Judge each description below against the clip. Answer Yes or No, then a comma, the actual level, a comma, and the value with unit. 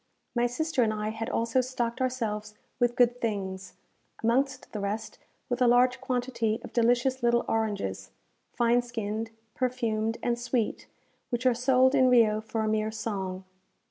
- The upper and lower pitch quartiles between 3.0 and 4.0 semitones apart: No, narrow, 2.5 semitones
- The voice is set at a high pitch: Yes, high, 235 Hz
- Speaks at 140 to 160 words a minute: Yes, average, 155 wpm